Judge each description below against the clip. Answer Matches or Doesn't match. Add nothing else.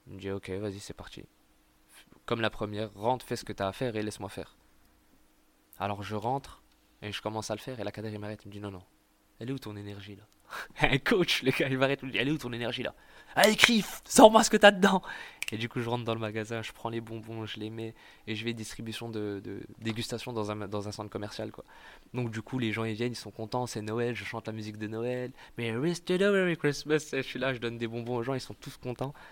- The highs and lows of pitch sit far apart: Doesn't match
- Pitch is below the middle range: Matches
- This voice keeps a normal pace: Doesn't match